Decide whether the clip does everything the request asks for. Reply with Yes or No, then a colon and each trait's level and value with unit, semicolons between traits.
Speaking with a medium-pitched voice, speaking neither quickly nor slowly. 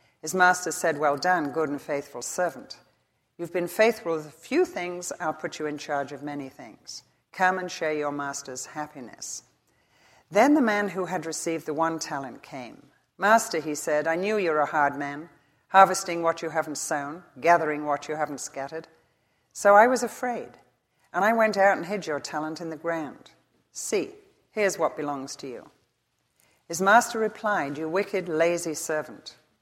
Yes: medium, 160 Hz; average, 175 wpm